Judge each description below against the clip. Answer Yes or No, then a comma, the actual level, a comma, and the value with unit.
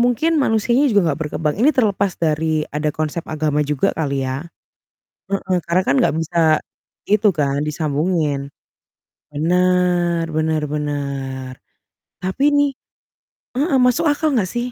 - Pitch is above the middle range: No, medium, 160 Hz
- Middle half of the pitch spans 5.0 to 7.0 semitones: Yes, wide, 5.5 semitones